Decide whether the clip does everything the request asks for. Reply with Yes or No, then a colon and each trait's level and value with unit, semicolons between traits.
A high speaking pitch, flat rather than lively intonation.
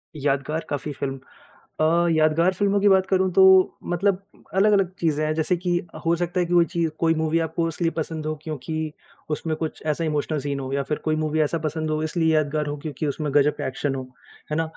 No: medium, 155 Hz; narrow, 2.2 semitones